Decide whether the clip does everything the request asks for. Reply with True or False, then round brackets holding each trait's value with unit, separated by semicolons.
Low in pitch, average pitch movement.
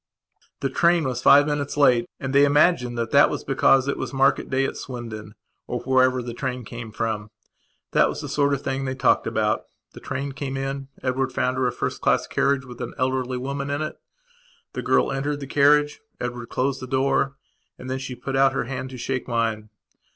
False (130 Hz; 2.0 semitones)